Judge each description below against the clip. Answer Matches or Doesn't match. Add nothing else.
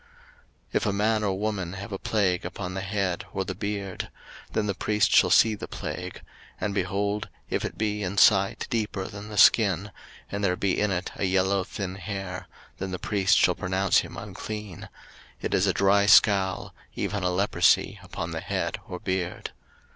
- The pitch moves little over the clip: Matches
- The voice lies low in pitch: Matches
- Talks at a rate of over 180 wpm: Matches